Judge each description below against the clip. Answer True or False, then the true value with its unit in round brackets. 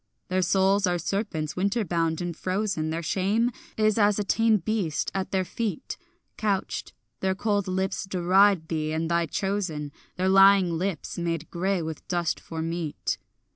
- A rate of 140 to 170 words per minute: True (155 wpm)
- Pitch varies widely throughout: False (3.2 semitones)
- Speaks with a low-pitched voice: False (185 Hz)